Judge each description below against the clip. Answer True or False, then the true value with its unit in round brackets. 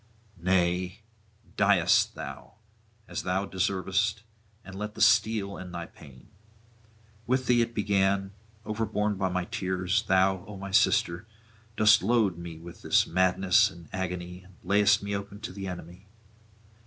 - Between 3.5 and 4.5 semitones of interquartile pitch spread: False (2.5 semitones)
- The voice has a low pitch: True (95 Hz)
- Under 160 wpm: True (140 wpm)